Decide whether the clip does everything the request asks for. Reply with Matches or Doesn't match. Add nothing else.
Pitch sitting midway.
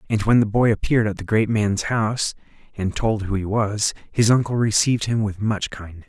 Doesn't match